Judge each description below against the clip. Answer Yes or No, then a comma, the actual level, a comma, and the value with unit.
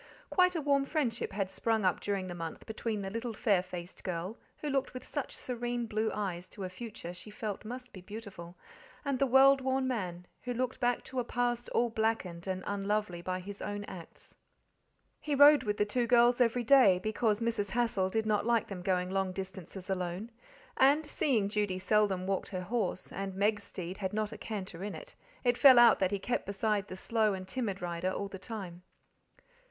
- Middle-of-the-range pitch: No, high, 210 Hz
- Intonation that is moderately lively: Yes, average, 4.3 semitones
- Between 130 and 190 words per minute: No, average, 200 wpm